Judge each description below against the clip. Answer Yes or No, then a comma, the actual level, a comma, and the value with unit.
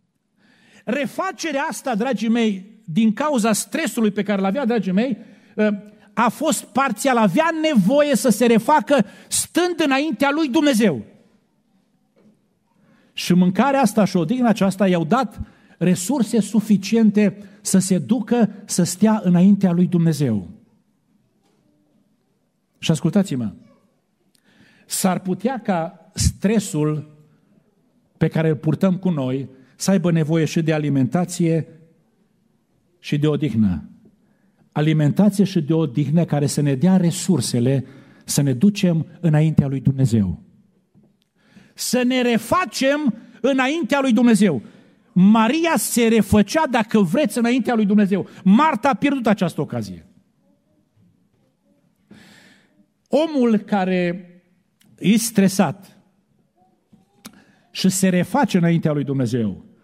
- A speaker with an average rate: No, slow, 105 wpm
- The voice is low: No, high, 205 Hz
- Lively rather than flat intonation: No, average, 4.6 semitones